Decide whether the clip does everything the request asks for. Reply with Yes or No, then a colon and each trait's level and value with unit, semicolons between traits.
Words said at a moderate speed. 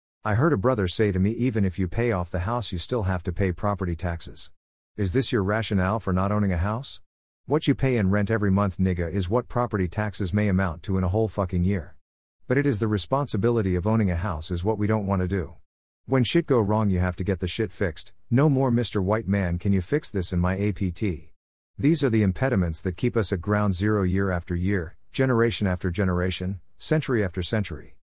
No: fast, 230 wpm